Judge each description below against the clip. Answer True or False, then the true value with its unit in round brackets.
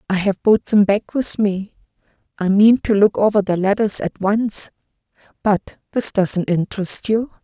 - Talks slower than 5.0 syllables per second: True (4.4 syllables/s)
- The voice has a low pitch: False (205 Hz)